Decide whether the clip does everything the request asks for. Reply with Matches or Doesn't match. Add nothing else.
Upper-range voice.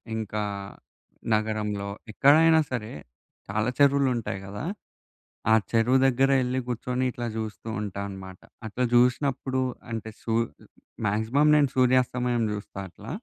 Doesn't match